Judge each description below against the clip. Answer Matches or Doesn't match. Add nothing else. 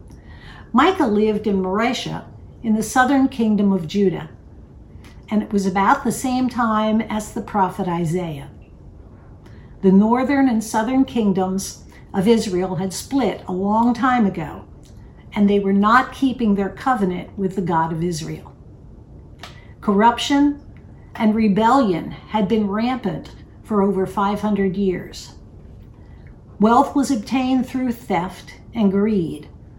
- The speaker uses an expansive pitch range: Doesn't match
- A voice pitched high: Matches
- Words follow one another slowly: Matches